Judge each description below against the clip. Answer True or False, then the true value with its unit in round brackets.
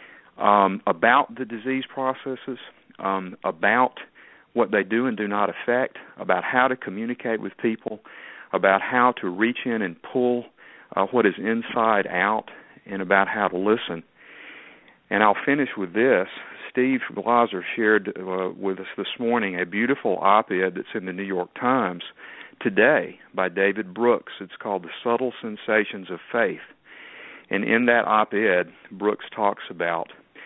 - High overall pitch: False (110 Hz)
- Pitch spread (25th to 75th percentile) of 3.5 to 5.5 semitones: True (4.0 semitones)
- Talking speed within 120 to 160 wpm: True (155 wpm)